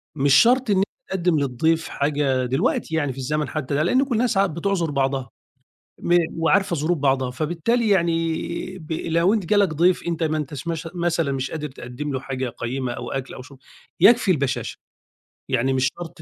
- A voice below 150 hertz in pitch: No, medium, 155 Hz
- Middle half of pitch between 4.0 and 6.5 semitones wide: Yes, average, 4.4 semitones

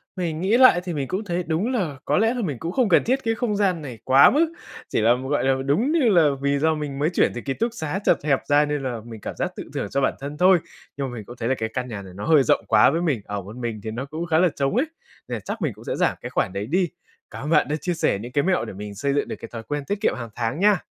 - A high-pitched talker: No, medium, 150 Hz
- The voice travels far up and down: Yes, wide, 6.8 semitones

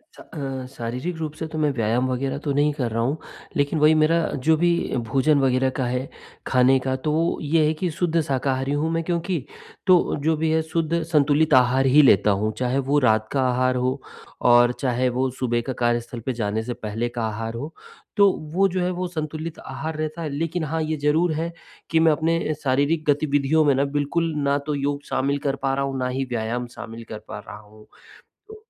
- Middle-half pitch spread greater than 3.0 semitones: Yes, average, 3.9 semitones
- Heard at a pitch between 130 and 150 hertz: Yes, medium, 140 Hz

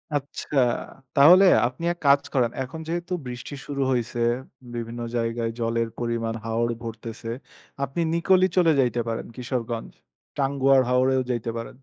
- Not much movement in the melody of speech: No, average, 3.1 semitones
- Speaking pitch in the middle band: No, low, 125 Hz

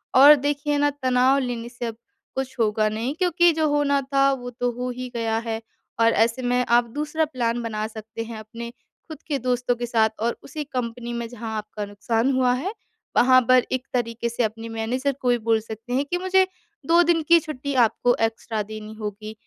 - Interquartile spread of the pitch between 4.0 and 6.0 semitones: No, average, 3.3 semitones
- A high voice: Yes, high, 245 Hz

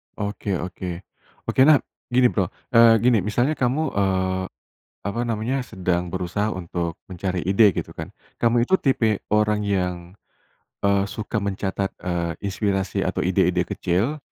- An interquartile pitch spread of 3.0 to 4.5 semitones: Yes, average, 3.6 semitones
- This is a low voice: Yes, low, 100 Hz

